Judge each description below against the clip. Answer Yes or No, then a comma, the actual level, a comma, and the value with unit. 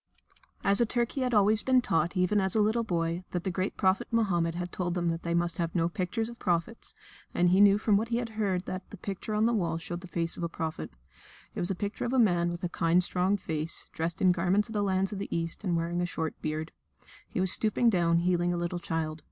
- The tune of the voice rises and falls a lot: No, average, 3.3 semitones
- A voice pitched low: No, medium, 180 Hz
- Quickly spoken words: Yes, fast, 255 wpm